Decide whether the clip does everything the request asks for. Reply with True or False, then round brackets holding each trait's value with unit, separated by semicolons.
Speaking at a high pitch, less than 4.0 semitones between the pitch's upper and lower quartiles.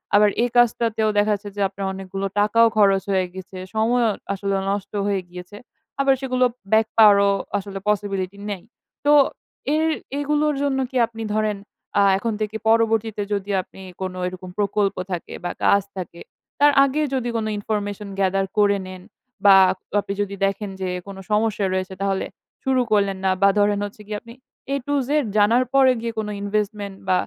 True (205 Hz; 2.4 semitones)